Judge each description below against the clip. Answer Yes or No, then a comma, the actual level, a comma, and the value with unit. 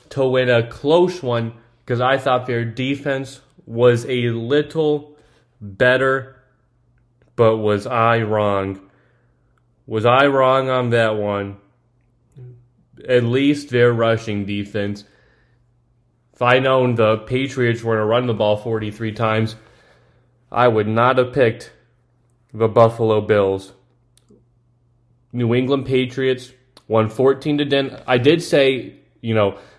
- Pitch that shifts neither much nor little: No, narrow, 2.2 semitones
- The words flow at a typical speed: No, slow, 125 wpm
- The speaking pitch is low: Yes, low, 120 Hz